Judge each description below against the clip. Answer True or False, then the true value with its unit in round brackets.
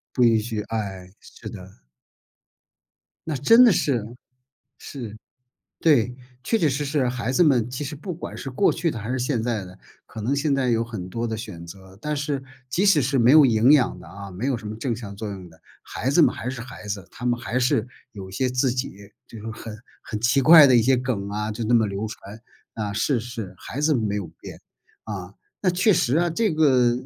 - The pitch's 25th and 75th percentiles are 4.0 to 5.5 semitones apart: True (4.4 semitones)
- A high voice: False (120 Hz)